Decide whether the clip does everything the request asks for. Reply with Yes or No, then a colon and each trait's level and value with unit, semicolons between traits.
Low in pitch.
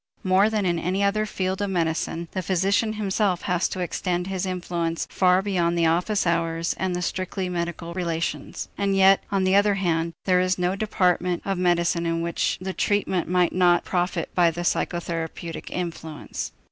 No: medium, 180 Hz